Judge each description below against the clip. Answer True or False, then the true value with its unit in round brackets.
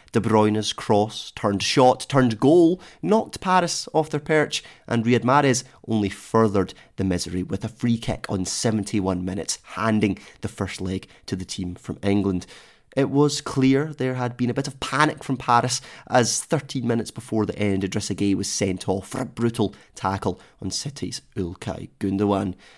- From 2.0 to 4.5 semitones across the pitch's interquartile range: False (5.0 semitones)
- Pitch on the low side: True (115 Hz)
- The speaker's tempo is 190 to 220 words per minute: False (175 wpm)